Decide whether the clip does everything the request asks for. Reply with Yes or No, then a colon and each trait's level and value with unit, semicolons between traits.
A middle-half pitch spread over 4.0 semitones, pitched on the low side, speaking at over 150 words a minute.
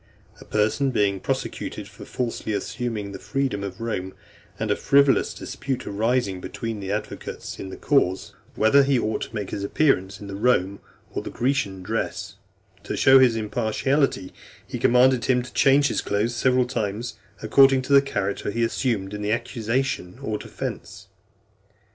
Yes: average, 4.4 semitones; low, 115 Hz; average, 160 wpm